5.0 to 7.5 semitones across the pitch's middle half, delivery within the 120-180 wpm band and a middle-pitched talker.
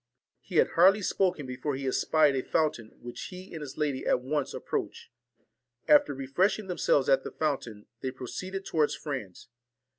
Yes: wide, 5.4 semitones; average, 170 wpm; medium, 145 Hz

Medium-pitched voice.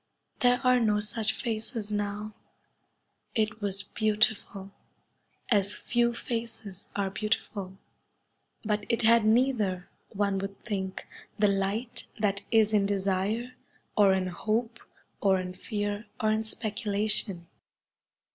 No: high, 210 Hz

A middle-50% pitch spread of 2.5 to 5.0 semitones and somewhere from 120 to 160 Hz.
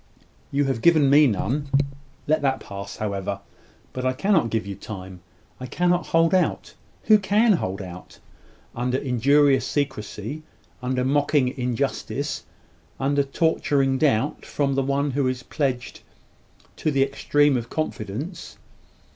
Yes: average, 3.1 semitones; low, 135 Hz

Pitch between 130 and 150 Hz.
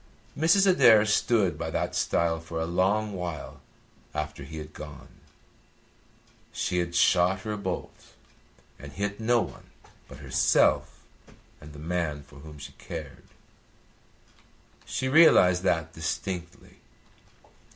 No: very low, 90 Hz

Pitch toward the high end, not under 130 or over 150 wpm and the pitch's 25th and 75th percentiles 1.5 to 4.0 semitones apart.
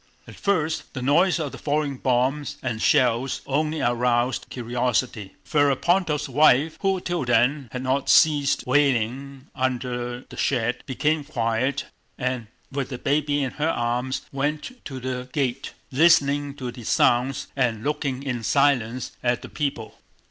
No: low, 135 Hz; average, 145 wpm; average, 3.0 semitones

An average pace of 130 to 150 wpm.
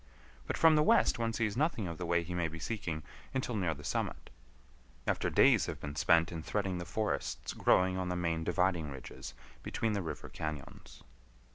No: average, 190 wpm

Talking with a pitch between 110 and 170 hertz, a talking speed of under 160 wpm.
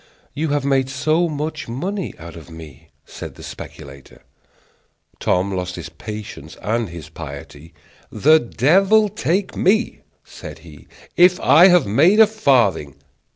Yes: low, 135 Hz; average, 140 wpm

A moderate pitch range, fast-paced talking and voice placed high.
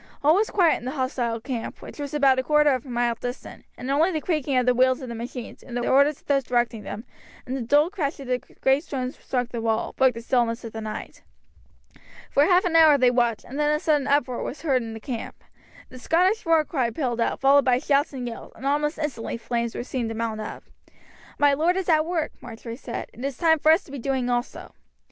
Yes: average, 3.7 semitones; fast, 240 wpm; very high, 265 Hz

